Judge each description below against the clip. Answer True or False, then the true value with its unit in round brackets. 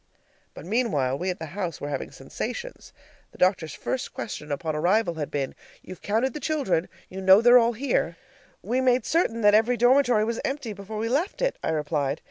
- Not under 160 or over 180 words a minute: False (195 wpm)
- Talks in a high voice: True (210 Hz)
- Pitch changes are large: True (7.2 semitones)